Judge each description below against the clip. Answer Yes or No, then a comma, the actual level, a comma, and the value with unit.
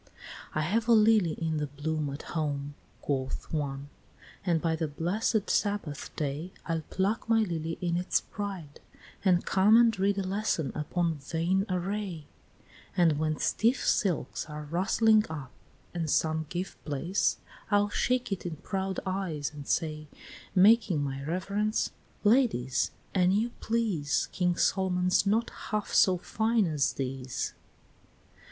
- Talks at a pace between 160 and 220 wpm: No, average, 145 wpm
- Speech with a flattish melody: No, average, 4.9 semitones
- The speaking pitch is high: No, medium, 175 Hz